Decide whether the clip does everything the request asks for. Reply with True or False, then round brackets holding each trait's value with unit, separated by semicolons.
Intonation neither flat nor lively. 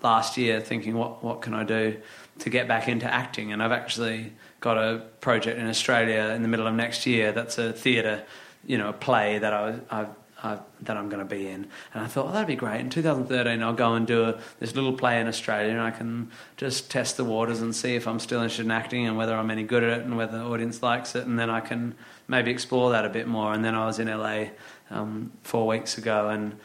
False (1.5 semitones)